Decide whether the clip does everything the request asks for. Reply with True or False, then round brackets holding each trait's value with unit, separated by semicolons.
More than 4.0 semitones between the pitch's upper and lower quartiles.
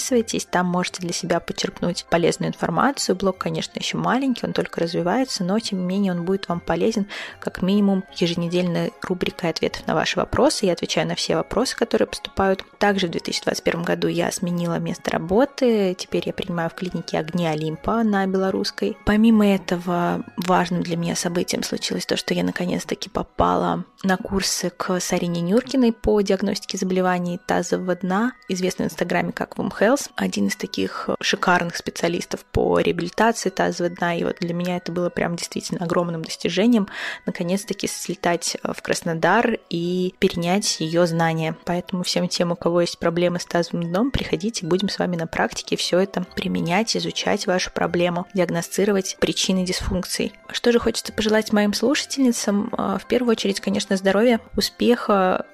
False (3.4 semitones)